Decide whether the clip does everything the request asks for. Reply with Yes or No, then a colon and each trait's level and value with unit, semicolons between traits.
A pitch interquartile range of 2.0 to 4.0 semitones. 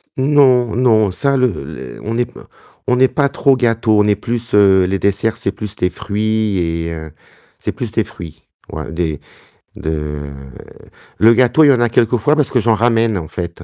No: average, 5.1 semitones